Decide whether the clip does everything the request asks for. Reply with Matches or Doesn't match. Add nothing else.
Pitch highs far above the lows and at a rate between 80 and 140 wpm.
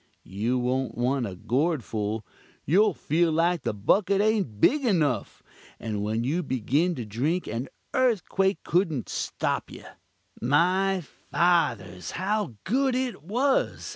Matches